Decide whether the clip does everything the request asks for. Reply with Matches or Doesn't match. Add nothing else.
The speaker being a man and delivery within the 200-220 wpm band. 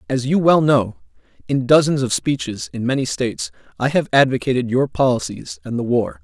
Doesn't match